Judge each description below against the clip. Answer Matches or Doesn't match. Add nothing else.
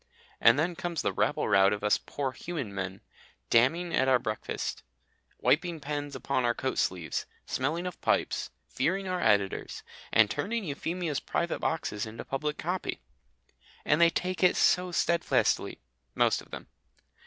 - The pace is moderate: Matches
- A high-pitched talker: Doesn't match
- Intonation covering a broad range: Matches